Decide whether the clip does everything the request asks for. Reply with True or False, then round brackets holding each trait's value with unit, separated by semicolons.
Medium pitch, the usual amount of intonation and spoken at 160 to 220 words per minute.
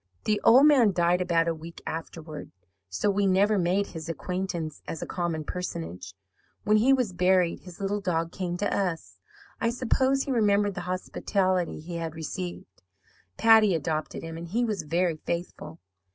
True (180 Hz; 3.7 semitones; 165 wpm)